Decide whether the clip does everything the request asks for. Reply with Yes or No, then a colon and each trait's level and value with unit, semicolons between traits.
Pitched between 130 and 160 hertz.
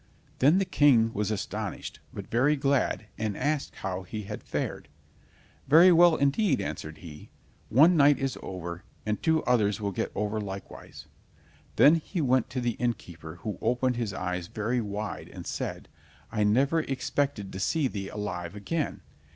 No: low, 115 Hz